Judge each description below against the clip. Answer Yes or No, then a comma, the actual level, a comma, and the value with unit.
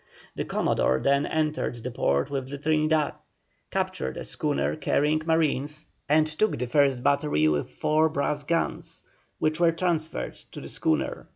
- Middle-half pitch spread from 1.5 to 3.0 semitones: Yes, average, 2.7 semitones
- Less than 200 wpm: Yes, average, 155 wpm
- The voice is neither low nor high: Yes, medium, 150 Hz